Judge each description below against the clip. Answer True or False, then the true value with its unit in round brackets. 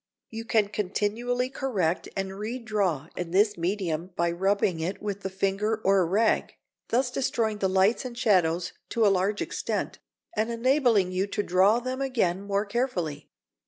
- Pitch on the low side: False (205 Hz)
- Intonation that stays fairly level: False (3.7 semitones)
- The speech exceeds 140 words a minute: True (160 wpm)